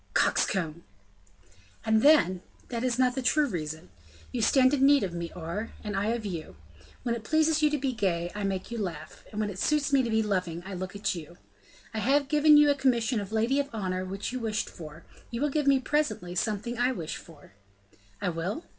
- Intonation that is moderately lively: No, wide, 6.4 semitones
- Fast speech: Yes, fast, 215 wpm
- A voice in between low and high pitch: No, high, 220 Hz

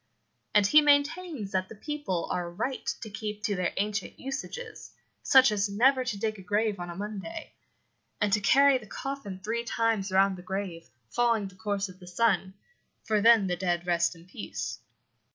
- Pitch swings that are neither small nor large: Yes, average, 3.9 semitones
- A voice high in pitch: Yes, high, 210 Hz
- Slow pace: No, average, 185 wpm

